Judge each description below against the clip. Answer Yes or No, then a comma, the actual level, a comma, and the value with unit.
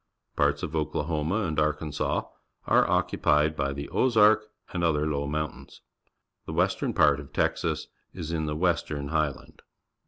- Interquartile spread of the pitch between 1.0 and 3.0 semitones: Yes, narrow, 2.5 semitones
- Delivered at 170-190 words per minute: No, average, 145 wpm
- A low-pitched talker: Yes, very low, 75 Hz